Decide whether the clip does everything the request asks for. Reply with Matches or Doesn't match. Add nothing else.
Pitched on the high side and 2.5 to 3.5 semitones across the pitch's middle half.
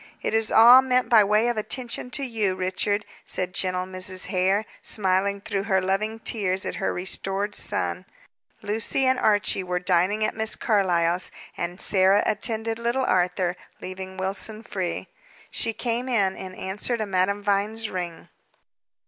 Matches